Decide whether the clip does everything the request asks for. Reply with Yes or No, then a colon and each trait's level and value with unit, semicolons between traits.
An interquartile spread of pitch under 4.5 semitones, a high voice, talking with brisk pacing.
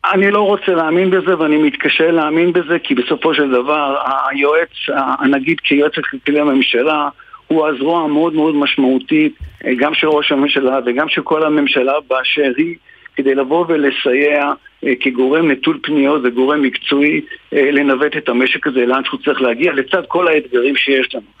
No: average, 3.3 semitones; medium, 150 Hz; fast, 155 wpm